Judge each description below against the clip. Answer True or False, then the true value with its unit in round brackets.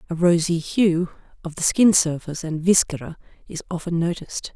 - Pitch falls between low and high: True (170 Hz)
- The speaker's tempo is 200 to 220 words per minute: False (160 wpm)